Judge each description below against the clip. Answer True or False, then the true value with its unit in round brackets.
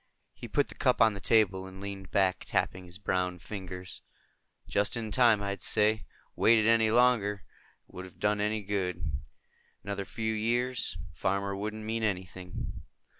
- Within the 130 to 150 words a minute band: False (165 wpm)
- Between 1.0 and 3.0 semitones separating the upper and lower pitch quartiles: True (2.7 semitones)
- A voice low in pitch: True (100 Hz)